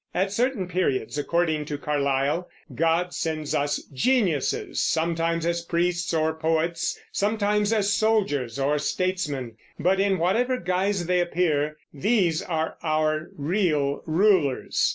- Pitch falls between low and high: Yes, medium, 170 Hz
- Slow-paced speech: Yes, slow, 125 wpm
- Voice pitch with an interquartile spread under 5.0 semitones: Yes, average, 3.9 semitones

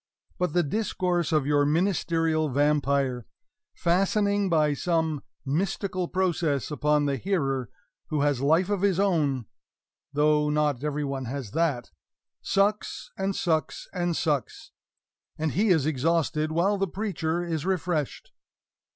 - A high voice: No, medium, 160 Hz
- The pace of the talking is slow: Yes, slow, 130 wpm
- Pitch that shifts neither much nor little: Yes, average, 3.9 semitones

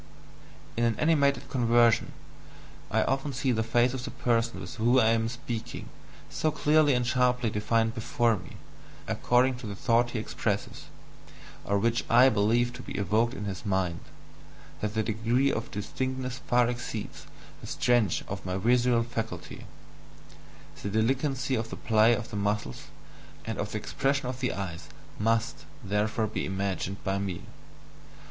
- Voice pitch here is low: Yes, low, 115 Hz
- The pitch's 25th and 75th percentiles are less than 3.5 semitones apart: Yes, average, 3.1 semitones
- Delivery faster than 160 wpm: No, average, 155 wpm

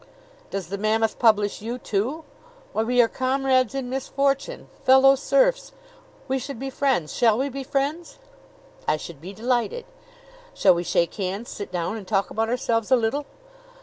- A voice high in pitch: Yes, high, 245 Hz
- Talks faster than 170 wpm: No, average, 165 wpm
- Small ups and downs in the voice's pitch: No, average, 4.6 semitones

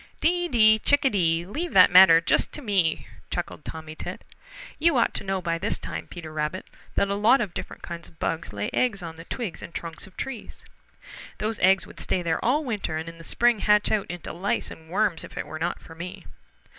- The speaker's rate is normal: No, fast, 220 wpm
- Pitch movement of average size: Yes, average, 4.7 semitones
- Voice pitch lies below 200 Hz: Yes, medium, 185 Hz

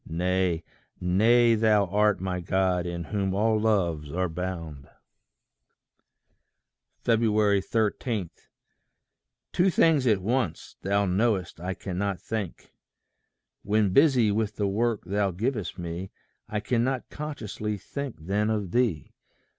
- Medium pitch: No, low, 100 Hz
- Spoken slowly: Yes, slow, 115 wpm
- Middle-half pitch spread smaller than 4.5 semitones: Yes, average, 3.5 semitones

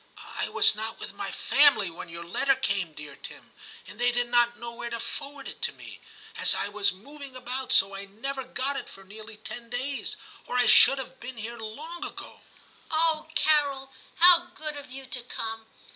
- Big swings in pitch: No, average, 4.2 semitones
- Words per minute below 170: No, fast, 205 wpm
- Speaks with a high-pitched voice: Yes, high, 245 Hz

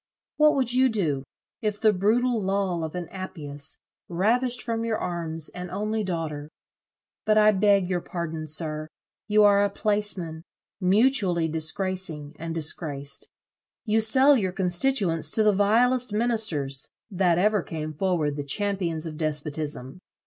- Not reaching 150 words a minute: Yes, average, 140 wpm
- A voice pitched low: No, medium, 185 Hz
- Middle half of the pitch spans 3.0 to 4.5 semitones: No, average, 5.0 semitones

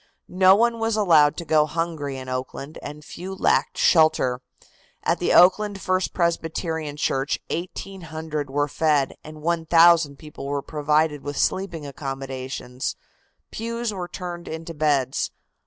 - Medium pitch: Yes, medium, 160 Hz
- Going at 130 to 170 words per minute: Yes, slow, 135 wpm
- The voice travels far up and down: No, average, 3.6 semitones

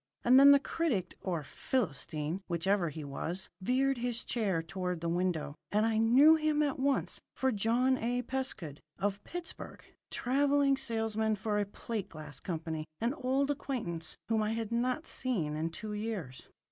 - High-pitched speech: Yes, high, 220 Hz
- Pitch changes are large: Yes, wide, 7.1 semitones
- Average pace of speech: Yes, average, 160 wpm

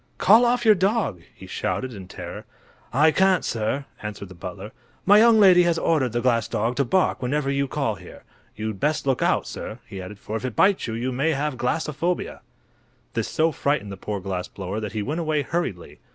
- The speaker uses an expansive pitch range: Yes, wide, 7.6 semitones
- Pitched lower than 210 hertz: Yes, low, 135 Hz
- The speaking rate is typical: No, fast, 210 wpm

